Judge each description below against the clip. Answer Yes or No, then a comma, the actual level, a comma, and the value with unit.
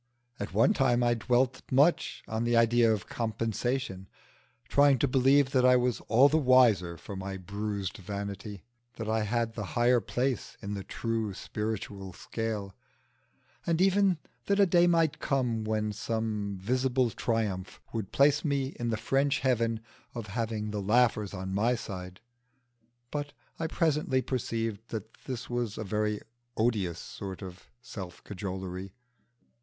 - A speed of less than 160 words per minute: Yes, average, 150 wpm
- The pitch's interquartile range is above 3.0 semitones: Yes, average, 4.1 semitones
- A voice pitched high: No, low, 115 Hz